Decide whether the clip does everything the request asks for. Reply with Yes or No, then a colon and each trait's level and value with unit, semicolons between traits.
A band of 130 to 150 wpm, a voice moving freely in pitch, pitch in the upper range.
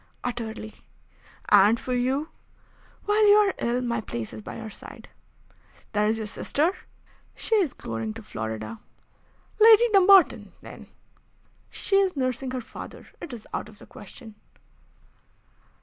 Yes: average, 140 wpm; wide, 8.5 semitones; high, 240 Hz